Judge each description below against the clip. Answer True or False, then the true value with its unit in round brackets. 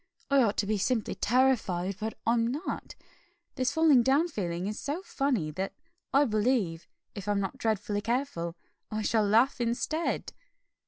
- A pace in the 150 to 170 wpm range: True (155 wpm)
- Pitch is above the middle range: True (225 Hz)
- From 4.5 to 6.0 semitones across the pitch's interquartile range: True (4.8 semitones)